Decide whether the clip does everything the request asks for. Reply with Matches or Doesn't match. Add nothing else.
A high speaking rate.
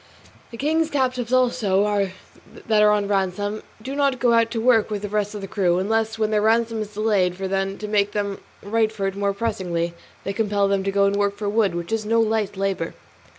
Matches